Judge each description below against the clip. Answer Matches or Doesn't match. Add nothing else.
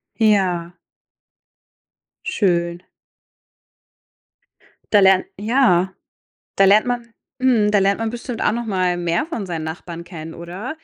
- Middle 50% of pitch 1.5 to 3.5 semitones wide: Doesn't match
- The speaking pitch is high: Matches